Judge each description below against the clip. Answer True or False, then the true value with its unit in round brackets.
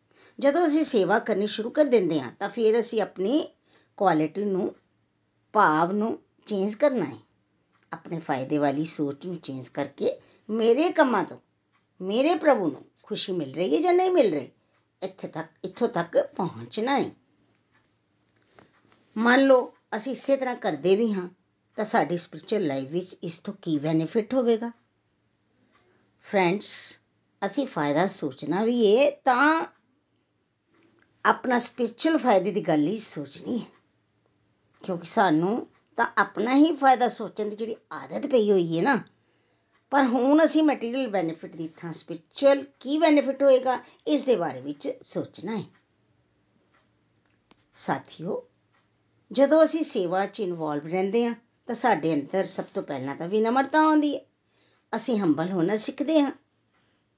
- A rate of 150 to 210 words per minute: False (140 wpm)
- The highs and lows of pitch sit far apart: True (7.8 semitones)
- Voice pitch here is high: True (215 Hz)